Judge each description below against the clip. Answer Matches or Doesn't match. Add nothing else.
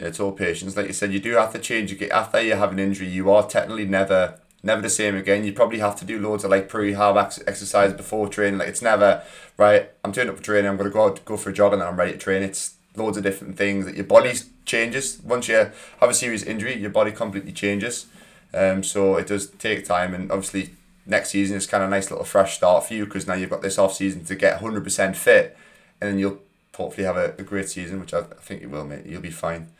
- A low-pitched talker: Matches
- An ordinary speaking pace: Doesn't match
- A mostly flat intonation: Matches